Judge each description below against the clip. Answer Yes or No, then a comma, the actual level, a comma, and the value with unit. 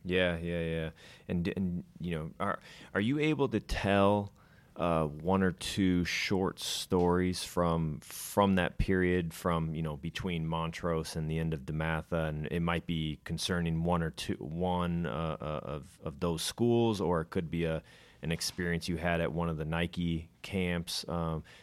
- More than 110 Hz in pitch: No, very low, 85 Hz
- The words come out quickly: No, average, 180 wpm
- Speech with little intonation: Yes, narrow, 2.0 semitones